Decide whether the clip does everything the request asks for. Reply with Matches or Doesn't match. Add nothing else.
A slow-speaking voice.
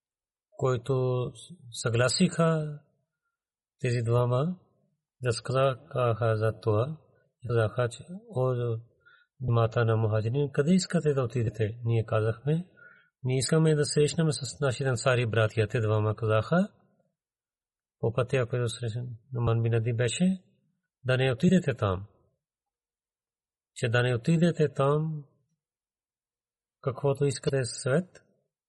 Matches